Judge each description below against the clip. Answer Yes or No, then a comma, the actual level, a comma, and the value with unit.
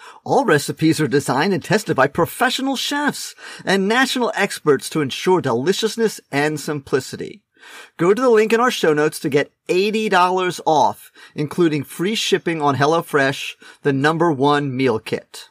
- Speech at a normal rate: Yes, average, 150 wpm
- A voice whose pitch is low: No, medium, 170 Hz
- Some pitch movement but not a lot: No, wide, 6.5 semitones